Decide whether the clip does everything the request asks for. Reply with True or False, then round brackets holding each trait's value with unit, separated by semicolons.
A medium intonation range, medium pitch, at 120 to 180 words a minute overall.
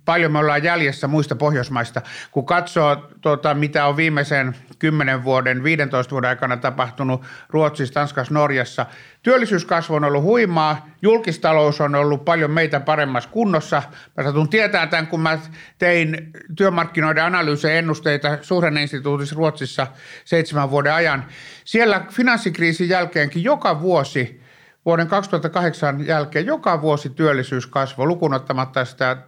True (3.1 semitones; 150 Hz; 125 wpm)